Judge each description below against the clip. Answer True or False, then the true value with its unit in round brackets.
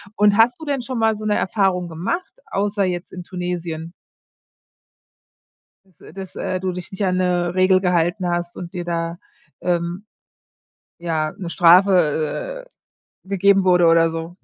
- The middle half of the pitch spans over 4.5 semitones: False (2.4 semitones)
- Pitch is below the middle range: False (180 Hz)